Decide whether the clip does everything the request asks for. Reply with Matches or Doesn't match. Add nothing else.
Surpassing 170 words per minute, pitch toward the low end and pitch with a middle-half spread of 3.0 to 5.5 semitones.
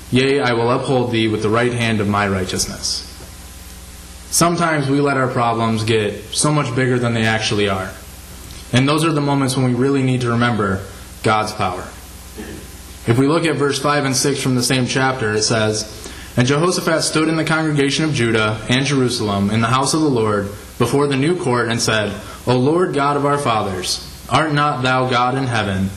Matches